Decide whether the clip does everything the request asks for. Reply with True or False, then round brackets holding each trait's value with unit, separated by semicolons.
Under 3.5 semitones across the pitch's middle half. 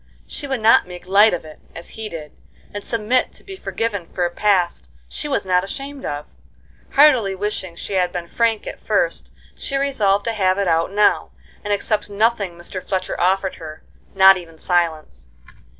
False (4.0 semitones)